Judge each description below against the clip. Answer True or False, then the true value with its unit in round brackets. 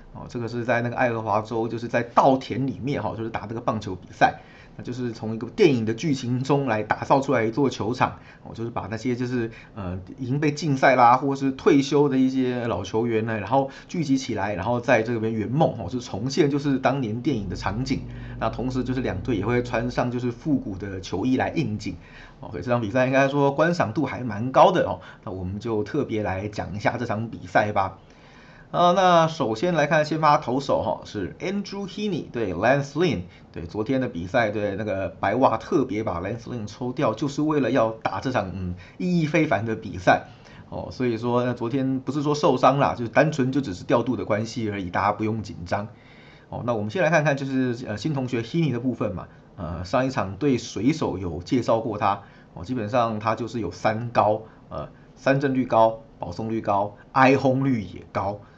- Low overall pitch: True (120 Hz)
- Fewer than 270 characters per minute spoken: False (335 characters per minute)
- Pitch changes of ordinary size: True (3.9 semitones)